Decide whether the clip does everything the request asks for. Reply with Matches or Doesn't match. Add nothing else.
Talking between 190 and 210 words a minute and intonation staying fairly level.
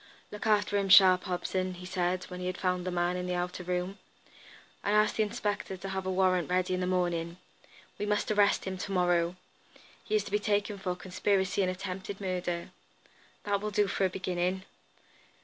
Matches